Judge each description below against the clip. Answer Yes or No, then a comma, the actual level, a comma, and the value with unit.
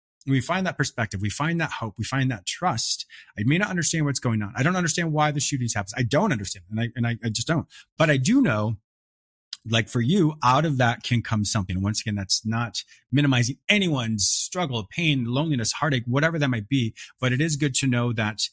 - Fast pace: Yes, fast, 225 wpm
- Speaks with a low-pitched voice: Yes, low, 125 Hz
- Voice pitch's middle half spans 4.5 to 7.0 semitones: Yes, average, 5.1 semitones